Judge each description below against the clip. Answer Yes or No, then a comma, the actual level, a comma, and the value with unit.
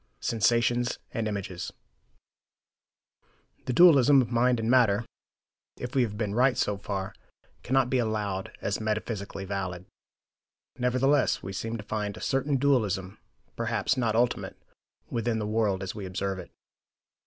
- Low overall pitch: Yes, low, 110 Hz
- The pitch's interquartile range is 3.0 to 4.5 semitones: Yes, average, 3.8 semitones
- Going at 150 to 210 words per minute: No, average, 140 wpm